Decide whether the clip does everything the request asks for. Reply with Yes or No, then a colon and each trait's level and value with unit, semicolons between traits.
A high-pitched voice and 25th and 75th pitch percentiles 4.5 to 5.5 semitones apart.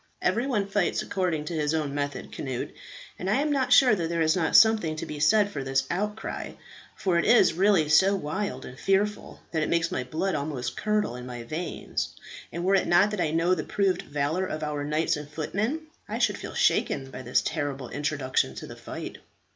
No: medium, 165 Hz; average, 5.1 semitones